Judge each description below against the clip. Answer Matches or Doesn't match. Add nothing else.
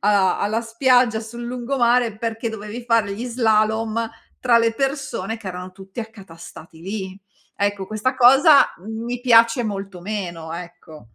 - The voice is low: Doesn't match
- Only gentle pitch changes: Doesn't match